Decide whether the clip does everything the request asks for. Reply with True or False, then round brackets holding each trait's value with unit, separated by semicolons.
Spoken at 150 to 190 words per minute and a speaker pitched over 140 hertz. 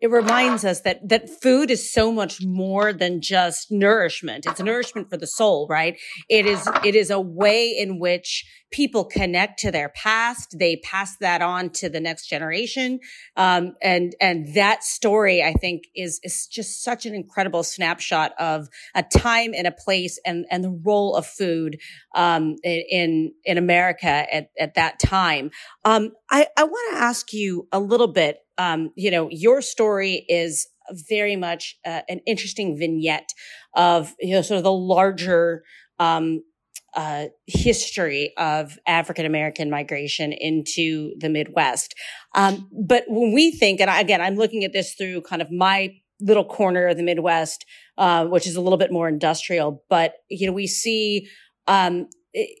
True (170 wpm; 185 Hz)